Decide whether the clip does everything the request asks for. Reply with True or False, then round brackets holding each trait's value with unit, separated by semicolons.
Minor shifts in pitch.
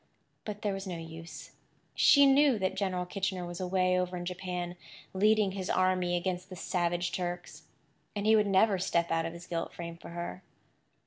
True (1.8 semitones)